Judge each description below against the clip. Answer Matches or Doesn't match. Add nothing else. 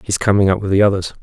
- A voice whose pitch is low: Matches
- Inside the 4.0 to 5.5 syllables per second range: Doesn't match